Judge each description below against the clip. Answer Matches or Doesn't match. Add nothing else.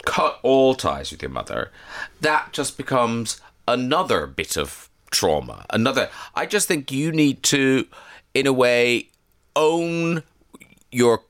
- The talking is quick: Doesn't match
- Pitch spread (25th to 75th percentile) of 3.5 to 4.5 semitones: Matches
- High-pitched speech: Doesn't match